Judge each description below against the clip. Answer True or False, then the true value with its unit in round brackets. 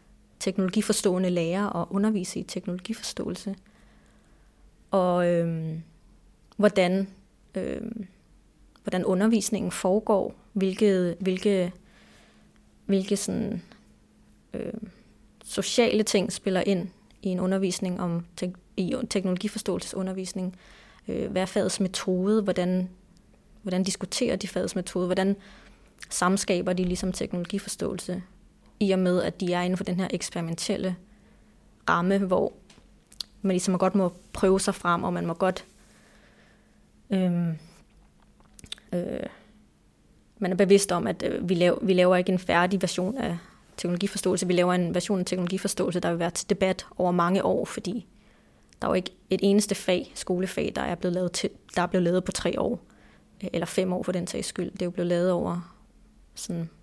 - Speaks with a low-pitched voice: False (185 Hz)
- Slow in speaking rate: True (140 wpm)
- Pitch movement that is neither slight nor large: False (1.8 semitones)